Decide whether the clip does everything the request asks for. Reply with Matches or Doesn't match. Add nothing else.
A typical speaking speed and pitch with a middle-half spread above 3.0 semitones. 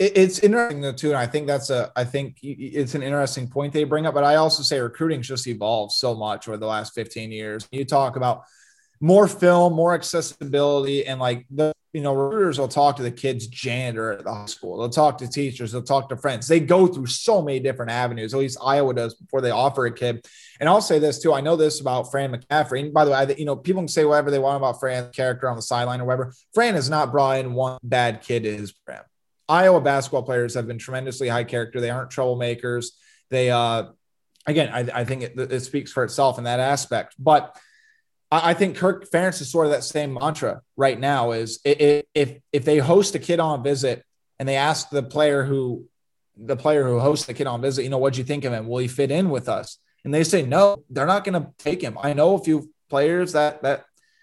Doesn't match